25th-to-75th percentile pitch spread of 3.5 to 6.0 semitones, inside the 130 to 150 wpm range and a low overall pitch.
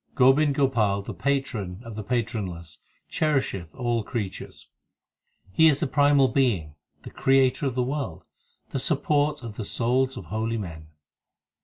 Yes: average, 5.1 semitones; average, 145 wpm; low, 125 Hz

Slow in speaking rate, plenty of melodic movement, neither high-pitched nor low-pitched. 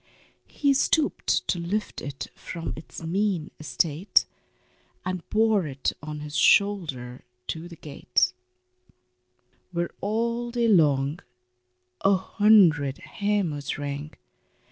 Yes: slow, 105 wpm; wide, 5.8 semitones; medium, 170 Hz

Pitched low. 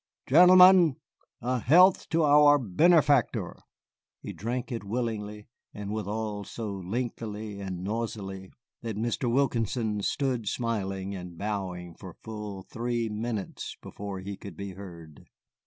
Yes: low, 110 Hz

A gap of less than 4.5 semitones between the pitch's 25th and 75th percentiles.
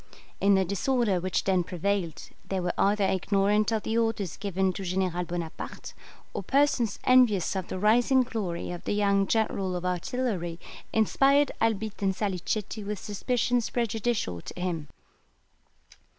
Yes: average, 3.6 semitones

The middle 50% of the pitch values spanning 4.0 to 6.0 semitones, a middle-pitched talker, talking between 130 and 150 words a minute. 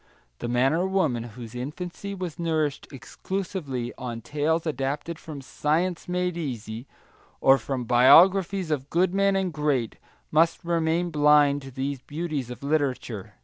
Yes: average, 4.9 semitones; medium, 150 Hz; average, 145 wpm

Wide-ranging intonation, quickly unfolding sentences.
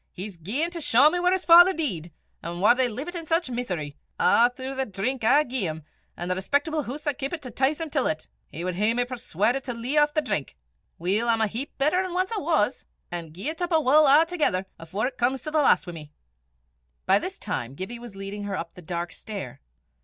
Yes: wide, 8.1 semitones; fast, 235 wpm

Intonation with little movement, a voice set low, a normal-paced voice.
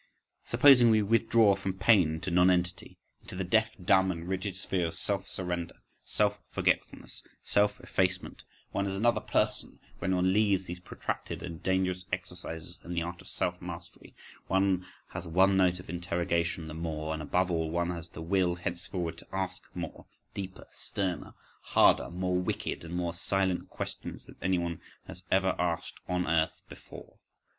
Yes: narrow, 1.9 semitones; very low, 90 Hz; average, 165 wpm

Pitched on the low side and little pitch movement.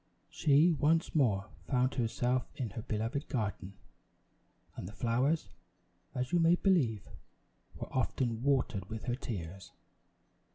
No: low, 125 Hz; average, 4.4 semitones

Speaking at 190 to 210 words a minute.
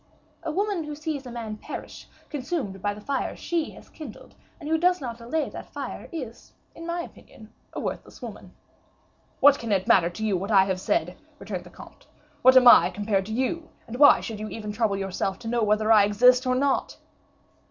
Yes: fast, 205 wpm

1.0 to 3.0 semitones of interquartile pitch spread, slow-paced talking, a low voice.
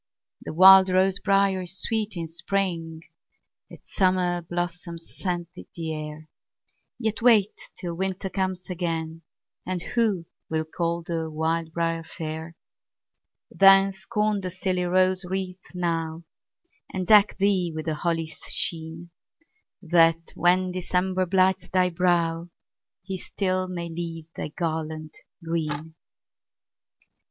No: narrow, 2.4 semitones; slow, 120 wpm; medium, 175 Hz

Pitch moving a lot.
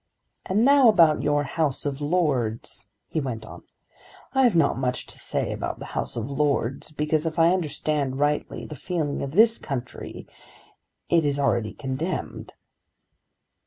No: average, 3.6 semitones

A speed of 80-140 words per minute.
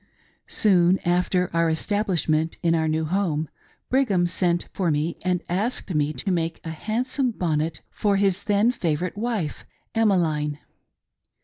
Yes: slow, 135 wpm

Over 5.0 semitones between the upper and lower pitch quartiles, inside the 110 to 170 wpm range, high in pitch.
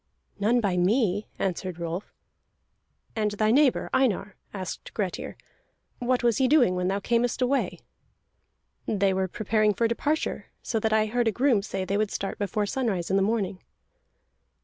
No: average, 3.7 semitones; average, 160 wpm; high, 210 Hz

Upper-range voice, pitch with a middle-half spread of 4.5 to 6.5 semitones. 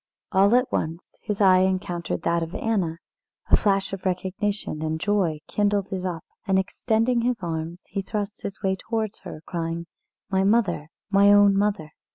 No: high, 195 Hz; average, 3.2 semitones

